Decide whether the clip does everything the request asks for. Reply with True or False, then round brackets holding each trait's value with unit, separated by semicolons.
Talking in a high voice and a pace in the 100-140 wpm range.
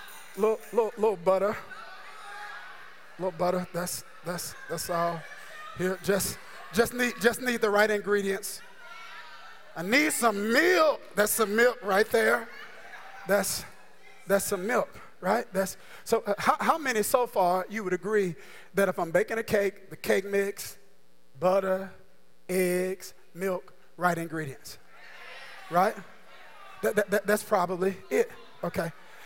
True (200 Hz; 135 wpm)